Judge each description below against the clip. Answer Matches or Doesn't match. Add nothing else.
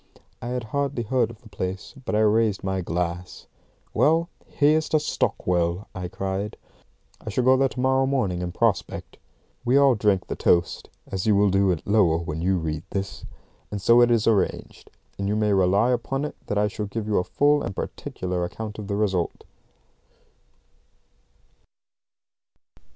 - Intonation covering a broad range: Doesn't match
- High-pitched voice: Doesn't match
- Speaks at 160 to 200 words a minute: Matches